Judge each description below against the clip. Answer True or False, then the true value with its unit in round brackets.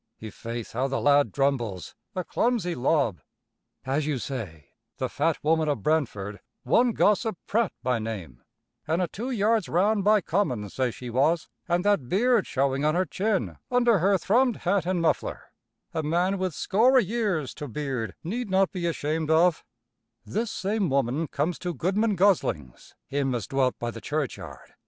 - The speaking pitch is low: False (160 Hz)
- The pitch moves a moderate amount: False (7.0 semitones)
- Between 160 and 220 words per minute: True (170 wpm)